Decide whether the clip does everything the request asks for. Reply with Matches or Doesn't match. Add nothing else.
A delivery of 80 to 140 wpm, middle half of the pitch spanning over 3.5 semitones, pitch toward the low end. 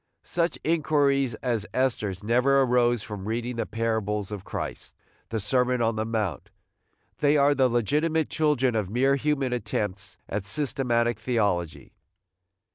Matches